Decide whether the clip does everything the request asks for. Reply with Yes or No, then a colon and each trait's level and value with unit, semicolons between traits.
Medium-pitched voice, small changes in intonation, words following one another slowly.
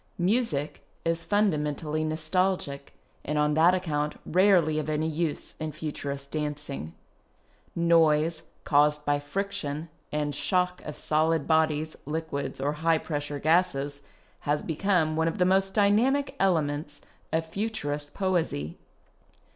No: medium, 155 Hz; average, 3.0 semitones; slow, 125 wpm